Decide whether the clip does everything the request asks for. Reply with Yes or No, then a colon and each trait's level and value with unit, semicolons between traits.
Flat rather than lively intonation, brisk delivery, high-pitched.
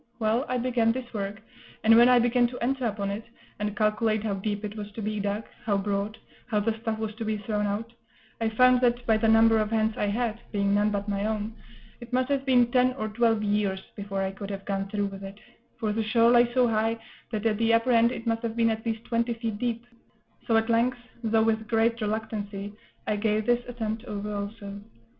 Yes: narrow, 2.0 semitones; fast, 230 wpm; high, 220 Hz